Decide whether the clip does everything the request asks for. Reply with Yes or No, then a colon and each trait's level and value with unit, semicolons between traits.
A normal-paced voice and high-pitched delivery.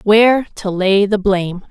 Yes: average, 175 wpm; high, 200 Hz